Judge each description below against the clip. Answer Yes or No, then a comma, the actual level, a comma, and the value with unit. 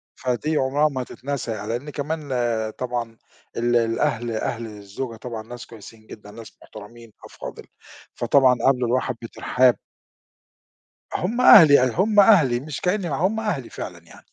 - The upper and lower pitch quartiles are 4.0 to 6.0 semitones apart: Yes, average, 4.4 semitones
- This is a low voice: Yes, low, 125 Hz